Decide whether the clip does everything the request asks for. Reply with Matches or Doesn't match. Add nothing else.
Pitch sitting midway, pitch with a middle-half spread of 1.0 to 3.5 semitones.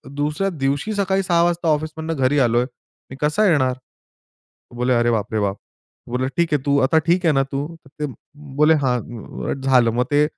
Doesn't match